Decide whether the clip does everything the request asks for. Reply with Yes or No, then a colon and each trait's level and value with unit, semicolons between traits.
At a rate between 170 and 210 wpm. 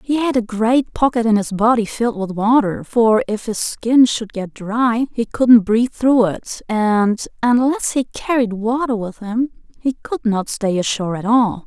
Yes: average, 190 wpm